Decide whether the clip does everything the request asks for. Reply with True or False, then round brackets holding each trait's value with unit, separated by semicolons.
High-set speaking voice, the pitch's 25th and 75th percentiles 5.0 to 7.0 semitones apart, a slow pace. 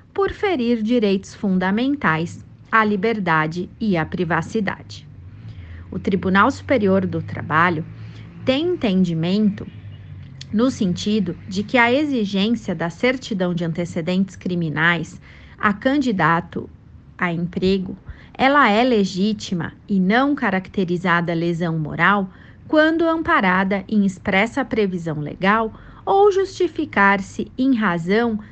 True (195 Hz; 5.3 semitones; 105 wpm)